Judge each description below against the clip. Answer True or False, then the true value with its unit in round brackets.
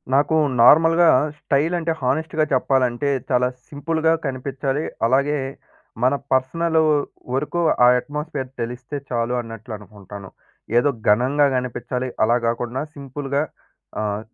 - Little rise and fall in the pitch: False (3.4 semitones)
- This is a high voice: False (135 Hz)